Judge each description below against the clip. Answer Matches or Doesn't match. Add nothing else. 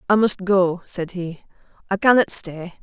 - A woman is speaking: Matches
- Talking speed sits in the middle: Matches